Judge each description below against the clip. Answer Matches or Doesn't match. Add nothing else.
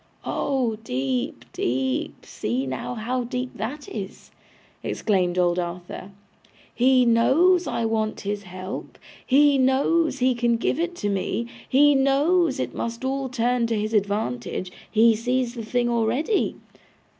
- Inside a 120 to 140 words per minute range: Matches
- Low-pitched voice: Doesn't match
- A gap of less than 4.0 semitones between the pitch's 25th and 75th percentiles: Doesn't match